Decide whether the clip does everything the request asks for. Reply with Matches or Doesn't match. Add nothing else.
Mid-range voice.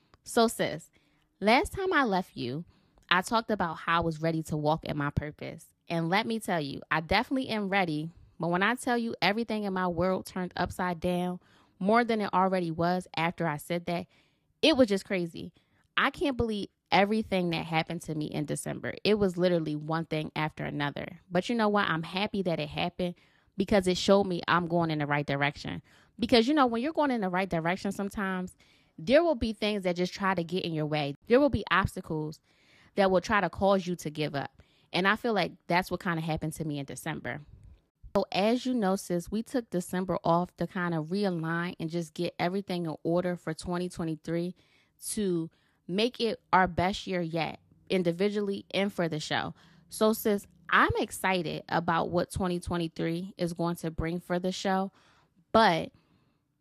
Matches